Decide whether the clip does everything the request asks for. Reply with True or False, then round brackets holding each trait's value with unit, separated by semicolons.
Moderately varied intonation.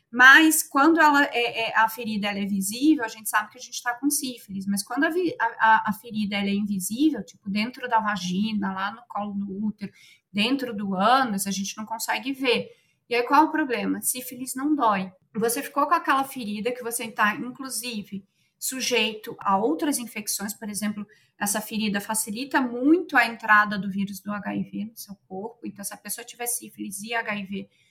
True (3.7 semitones)